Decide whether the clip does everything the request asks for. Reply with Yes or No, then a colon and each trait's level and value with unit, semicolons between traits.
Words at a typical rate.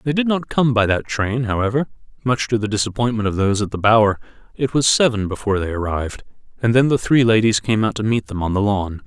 No: fast, 240 wpm